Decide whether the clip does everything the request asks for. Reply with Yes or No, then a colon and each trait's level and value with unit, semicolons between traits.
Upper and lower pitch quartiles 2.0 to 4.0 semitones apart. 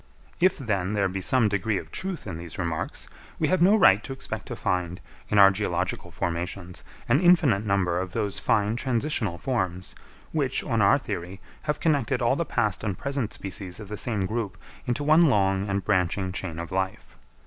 No: average, 5.2 semitones